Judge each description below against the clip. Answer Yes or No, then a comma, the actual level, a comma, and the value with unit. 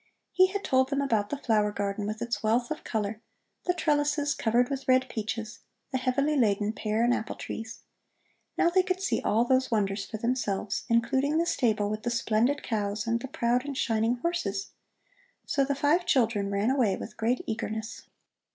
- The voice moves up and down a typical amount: Yes, average, 4.2 semitones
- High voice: Yes, high, 235 Hz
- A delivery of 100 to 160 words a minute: No, average, 185 wpm